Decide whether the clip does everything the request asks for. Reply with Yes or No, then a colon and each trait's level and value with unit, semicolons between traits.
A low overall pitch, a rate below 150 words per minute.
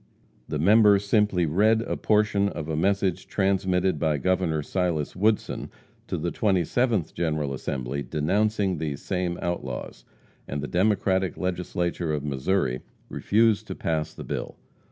Yes: very low, 90 Hz; slow, 135 wpm